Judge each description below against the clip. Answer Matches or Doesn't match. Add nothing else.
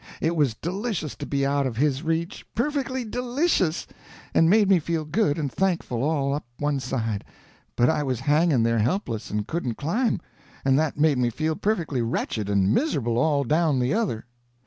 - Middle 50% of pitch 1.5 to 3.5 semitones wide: Doesn't match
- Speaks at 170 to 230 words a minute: Matches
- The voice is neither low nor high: Matches